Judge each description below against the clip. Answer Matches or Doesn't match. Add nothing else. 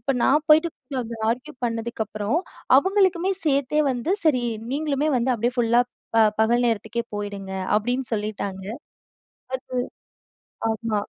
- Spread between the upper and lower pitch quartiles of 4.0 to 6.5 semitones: Matches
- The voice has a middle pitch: Doesn't match